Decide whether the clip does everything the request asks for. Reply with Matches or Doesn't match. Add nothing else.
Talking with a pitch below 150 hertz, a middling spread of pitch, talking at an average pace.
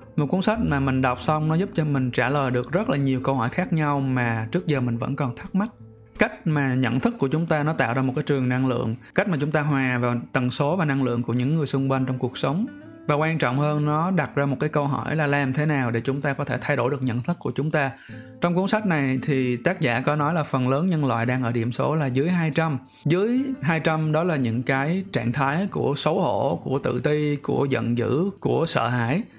Doesn't match